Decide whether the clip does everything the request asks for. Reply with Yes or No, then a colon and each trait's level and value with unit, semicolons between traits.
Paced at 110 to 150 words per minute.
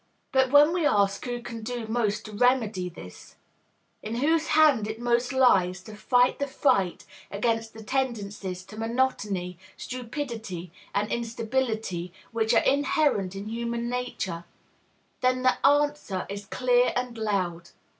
Yes: average, 140 wpm